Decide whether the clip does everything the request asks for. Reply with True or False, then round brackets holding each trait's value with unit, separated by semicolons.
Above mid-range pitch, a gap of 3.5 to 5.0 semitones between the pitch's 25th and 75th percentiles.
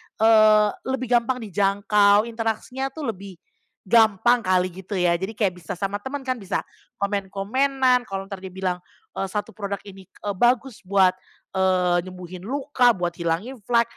True (205 Hz; 4.1 semitones)